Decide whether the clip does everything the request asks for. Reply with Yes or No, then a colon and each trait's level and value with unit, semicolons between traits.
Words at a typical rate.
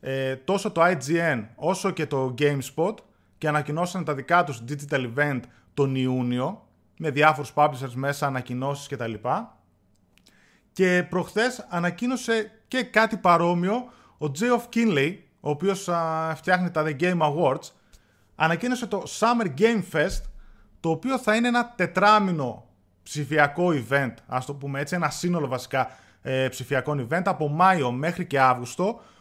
Yes: average, 140 wpm